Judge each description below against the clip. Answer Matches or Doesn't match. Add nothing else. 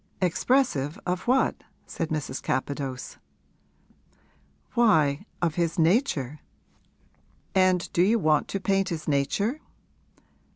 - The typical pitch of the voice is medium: Matches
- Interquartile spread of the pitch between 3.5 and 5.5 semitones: Matches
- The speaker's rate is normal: Doesn't match